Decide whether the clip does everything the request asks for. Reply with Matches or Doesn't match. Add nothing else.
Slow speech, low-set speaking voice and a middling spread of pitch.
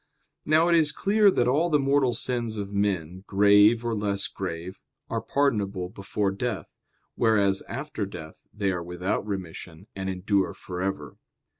Doesn't match